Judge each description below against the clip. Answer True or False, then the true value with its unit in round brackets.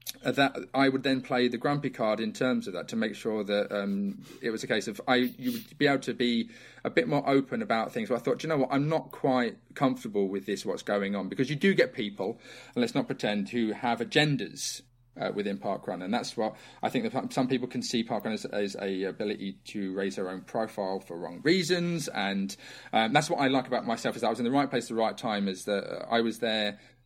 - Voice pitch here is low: True (120 Hz)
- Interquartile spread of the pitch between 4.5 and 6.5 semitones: True (4.8 semitones)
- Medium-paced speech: False (255 wpm)